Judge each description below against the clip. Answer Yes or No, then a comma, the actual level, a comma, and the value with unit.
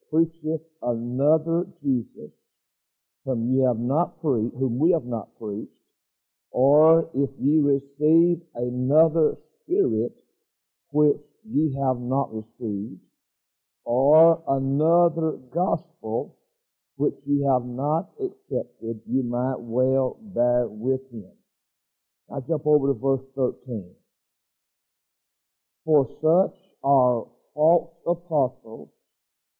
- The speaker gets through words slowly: Yes, slow, 100 wpm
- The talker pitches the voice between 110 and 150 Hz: Yes, medium, 140 Hz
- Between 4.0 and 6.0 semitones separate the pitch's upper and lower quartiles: Yes, average, 4.4 semitones